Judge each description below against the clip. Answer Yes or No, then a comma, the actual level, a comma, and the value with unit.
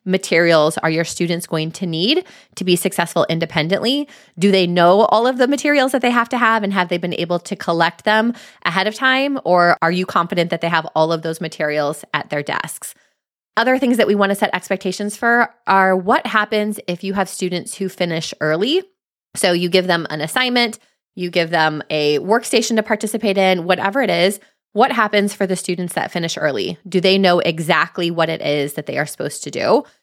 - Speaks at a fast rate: Yes, fast, 210 wpm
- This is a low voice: No, medium, 185 Hz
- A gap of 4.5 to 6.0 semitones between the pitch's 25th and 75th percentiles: No, average, 4.1 semitones